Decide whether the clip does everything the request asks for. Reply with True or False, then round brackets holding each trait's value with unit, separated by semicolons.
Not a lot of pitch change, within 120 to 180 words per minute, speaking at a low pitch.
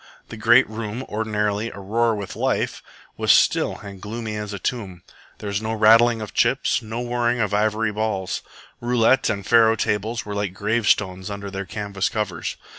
True (2.0 semitones; 170 wpm; 105 Hz)